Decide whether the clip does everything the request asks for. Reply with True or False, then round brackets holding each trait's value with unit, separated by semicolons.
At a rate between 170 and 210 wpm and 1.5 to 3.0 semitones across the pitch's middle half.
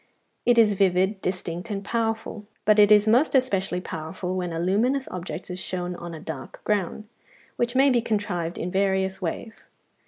False (175 wpm; 3.6 semitones)